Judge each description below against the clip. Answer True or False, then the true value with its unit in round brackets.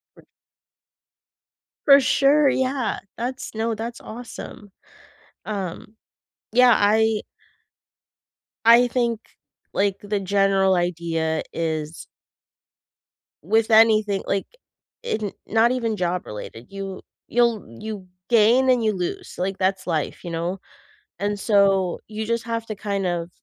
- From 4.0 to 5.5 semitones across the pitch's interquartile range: False (3.6 semitones)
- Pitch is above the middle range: True (210 Hz)